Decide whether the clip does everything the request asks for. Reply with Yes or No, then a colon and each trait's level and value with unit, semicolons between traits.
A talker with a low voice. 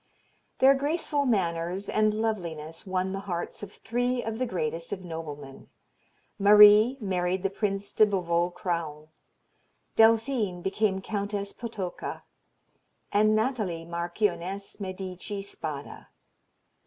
No: high, 195 Hz